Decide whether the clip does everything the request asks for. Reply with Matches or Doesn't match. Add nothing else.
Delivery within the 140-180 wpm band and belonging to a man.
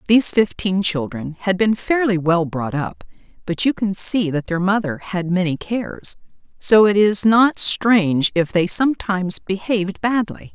Doesn't match